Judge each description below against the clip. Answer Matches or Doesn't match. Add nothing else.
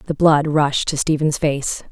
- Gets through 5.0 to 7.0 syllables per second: Doesn't match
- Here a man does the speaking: Doesn't match